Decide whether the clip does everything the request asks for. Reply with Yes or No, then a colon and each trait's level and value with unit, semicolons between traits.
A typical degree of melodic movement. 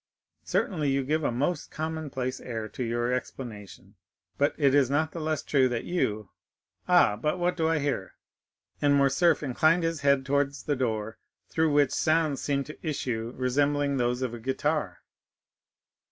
Yes: average, 3.8 semitones